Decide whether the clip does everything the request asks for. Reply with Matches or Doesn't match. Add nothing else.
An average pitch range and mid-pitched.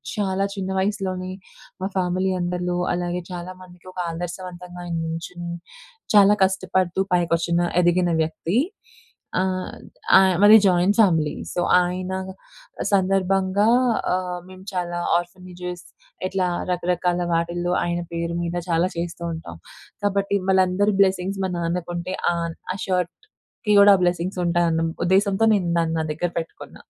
Doesn't match